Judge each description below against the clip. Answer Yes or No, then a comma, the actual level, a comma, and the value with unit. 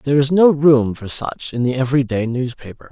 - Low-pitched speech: Yes, low, 130 Hz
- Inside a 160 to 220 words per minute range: Yes, fast, 205 wpm